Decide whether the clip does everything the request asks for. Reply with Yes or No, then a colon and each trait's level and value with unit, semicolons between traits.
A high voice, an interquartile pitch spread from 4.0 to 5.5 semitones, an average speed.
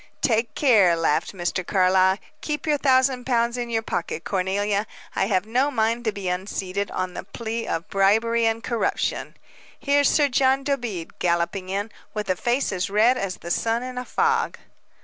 Yes: high, 220 Hz; average, 4.8 semitones; average, 175 wpm